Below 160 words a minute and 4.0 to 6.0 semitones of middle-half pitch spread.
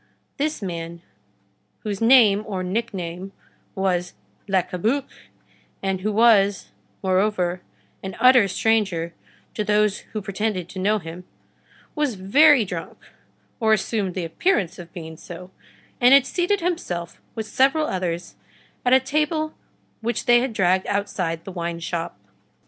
Yes: average, 140 wpm; average, 4.7 semitones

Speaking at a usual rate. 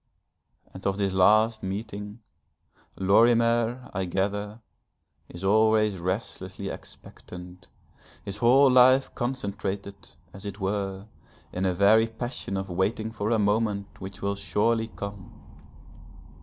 No: slow, 115 wpm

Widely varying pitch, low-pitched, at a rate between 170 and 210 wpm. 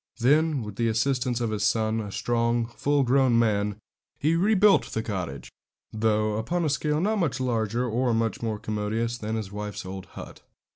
No: average, 3.7 semitones; low, 115 Hz; average, 185 wpm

